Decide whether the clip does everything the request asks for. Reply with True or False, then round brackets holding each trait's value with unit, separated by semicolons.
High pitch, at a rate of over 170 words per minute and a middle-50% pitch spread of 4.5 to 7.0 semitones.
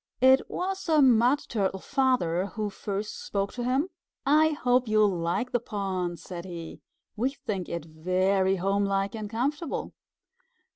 False (210 Hz; 145 wpm; 5.4 semitones)